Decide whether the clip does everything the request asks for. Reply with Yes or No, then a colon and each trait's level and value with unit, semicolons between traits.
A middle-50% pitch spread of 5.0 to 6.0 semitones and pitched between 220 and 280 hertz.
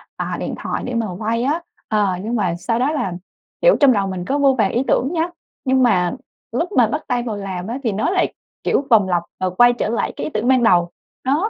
Yes: average, 5.3 semitones; high, 230 Hz